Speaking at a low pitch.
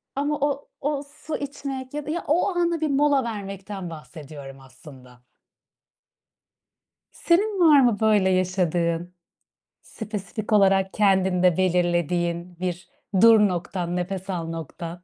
No: high, 190 Hz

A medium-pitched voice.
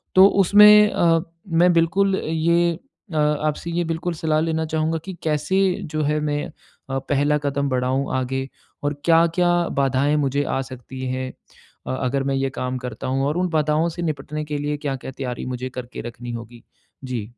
Yes: medium, 150 Hz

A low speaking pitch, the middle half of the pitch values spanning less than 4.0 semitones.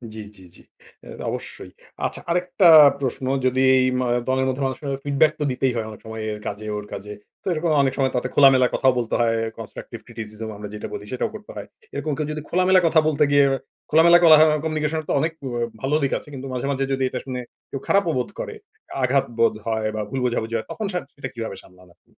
No: low, 130 Hz; average, 4.8 semitones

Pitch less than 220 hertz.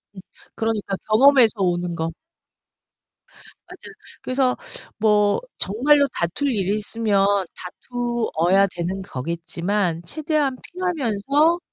Yes: high, 210 Hz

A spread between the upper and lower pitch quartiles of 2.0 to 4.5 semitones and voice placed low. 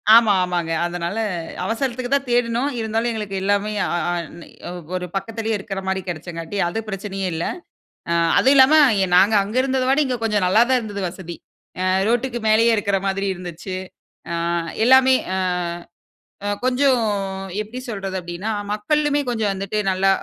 No: average, 4.2 semitones; high, 215 Hz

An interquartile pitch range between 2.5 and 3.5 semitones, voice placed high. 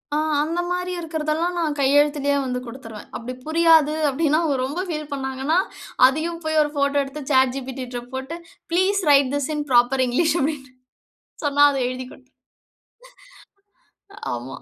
Yes: average, 3.2 semitones; very high, 285 Hz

